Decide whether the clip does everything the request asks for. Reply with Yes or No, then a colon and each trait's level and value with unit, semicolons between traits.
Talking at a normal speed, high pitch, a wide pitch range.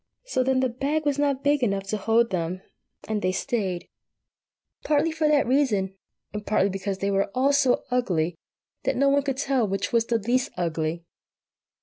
Yes: average, 185 wpm; high, 235 Hz; wide, 6.0 semitones